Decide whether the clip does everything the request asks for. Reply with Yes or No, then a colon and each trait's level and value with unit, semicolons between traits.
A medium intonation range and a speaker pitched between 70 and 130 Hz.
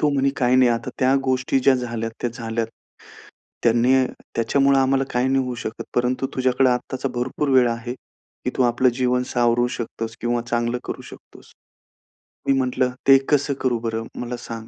No: narrow, 1.8 semitones; low, 125 Hz